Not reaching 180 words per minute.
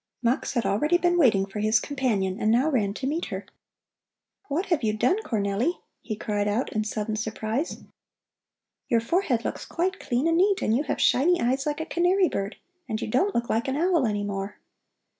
No: average, 195 wpm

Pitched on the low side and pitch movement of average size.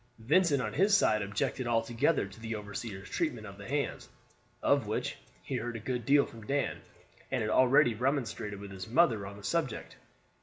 Yes: low, 115 Hz; average, 4.8 semitones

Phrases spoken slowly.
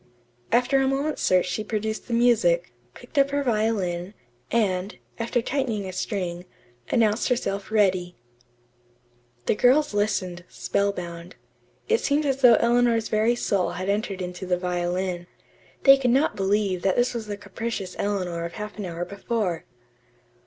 No: average, 150 wpm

